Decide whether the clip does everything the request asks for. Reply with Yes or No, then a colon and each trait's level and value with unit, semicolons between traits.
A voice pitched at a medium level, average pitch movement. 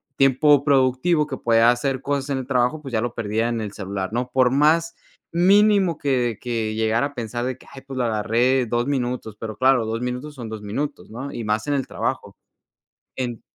No: low, 125 Hz; average, 3.5 semitones